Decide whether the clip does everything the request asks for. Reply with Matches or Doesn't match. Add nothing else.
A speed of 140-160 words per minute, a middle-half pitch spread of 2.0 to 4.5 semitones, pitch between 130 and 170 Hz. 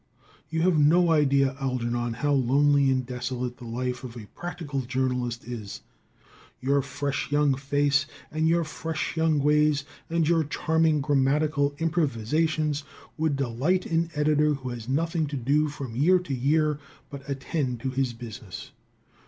Matches